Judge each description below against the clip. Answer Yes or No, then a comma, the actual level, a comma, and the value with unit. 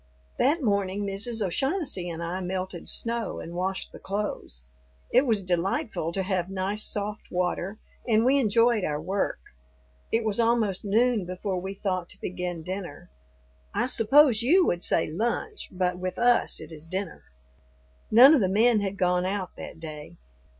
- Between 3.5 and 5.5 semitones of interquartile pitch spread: Yes, average, 4.2 semitones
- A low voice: No, high, 195 Hz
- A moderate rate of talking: Yes, average, 165 wpm